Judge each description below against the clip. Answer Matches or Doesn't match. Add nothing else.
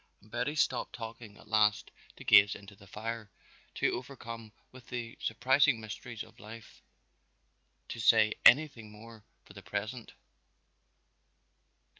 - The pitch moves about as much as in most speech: Doesn't match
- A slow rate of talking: Matches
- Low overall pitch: Matches